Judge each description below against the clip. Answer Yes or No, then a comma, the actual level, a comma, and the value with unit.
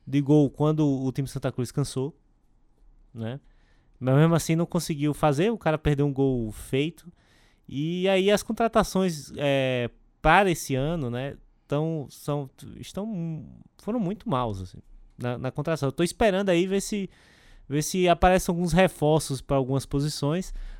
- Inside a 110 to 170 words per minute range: Yes, average, 155 wpm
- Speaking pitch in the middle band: Yes, medium, 150 Hz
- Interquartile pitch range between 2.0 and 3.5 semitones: No, average, 4.9 semitones